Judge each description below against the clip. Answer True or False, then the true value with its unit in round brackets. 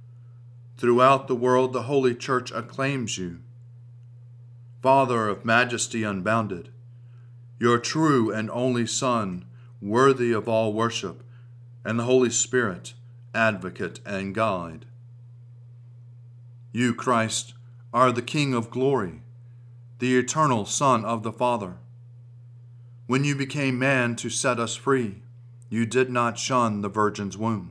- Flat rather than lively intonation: True (1.1 semitones)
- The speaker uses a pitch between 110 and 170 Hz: True (120 Hz)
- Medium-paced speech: False (120 wpm)